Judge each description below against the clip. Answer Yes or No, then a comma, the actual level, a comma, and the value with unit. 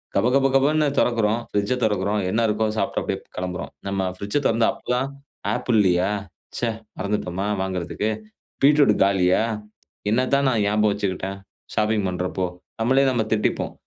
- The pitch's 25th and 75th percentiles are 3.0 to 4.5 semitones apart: Yes, average, 4.1 semitones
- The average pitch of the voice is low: Yes, low, 105 Hz